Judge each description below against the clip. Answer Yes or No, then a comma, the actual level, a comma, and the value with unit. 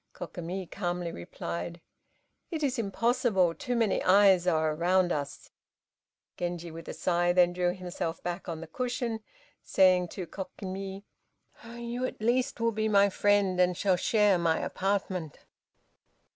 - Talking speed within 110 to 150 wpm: Yes, average, 140 wpm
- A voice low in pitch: No, medium, 185 Hz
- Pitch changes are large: No, average, 3.4 semitones